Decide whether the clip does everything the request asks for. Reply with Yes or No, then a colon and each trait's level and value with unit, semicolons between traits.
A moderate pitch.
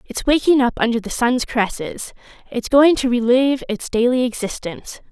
No: high, 245 Hz